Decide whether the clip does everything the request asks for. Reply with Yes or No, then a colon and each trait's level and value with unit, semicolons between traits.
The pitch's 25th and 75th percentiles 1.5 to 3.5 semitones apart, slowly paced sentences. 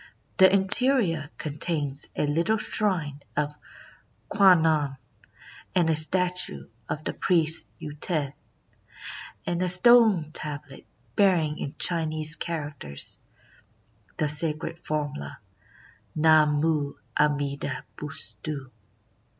Yes: average, 3.1 semitones; slow, 95 wpm